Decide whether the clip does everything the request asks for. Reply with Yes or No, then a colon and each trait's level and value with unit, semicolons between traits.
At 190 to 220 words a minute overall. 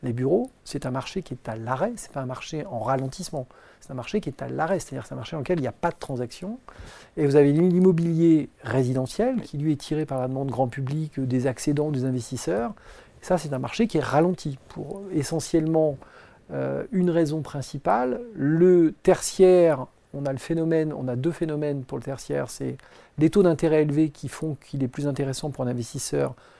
Yes: average, 210 wpm